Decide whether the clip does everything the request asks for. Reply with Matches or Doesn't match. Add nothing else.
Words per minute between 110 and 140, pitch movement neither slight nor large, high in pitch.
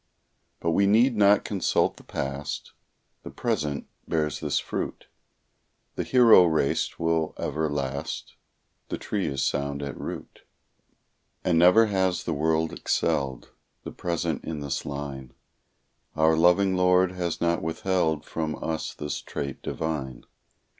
Doesn't match